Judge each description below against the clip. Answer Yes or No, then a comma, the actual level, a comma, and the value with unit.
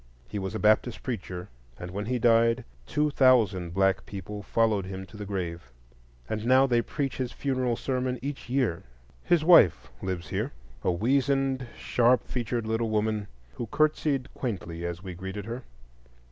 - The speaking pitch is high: No, low, 110 Hz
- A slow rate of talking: No, average, 160 wpm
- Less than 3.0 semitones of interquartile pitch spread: No, average, 5.0 semitones